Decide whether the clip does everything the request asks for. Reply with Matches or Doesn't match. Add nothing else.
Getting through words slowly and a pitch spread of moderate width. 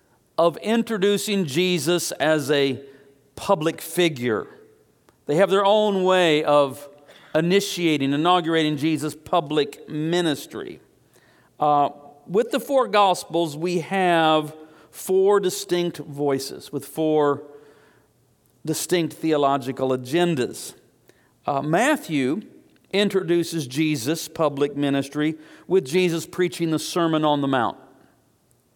Matches